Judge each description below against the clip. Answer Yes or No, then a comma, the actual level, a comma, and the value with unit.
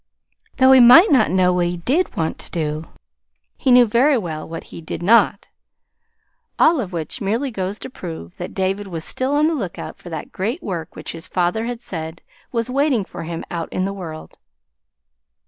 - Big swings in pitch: Yes, wide, 6.6 semitones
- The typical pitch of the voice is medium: No, high, 195 Hz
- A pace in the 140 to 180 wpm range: No, average, 195 wpm